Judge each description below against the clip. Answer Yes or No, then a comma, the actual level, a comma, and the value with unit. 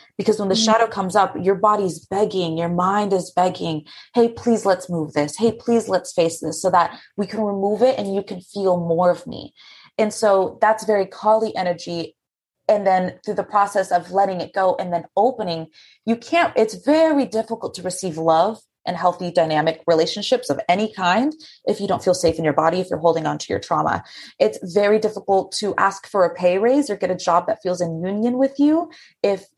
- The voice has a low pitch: No, high, 195 Hz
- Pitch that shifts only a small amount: No, average, 3.6 semitones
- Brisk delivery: Yes, fast, 210 wpm